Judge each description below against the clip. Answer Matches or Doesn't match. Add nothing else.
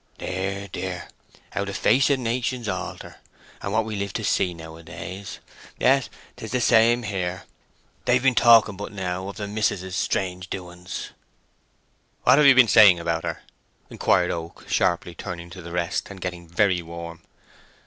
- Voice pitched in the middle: Doesn't match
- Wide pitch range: Doesn't match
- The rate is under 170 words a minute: Matches